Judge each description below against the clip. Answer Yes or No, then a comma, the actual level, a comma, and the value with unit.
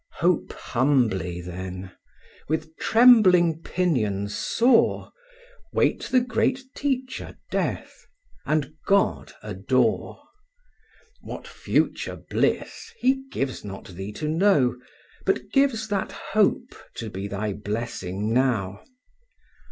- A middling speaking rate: No, slow, 100 wpm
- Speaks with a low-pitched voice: No, medium, 150 Hz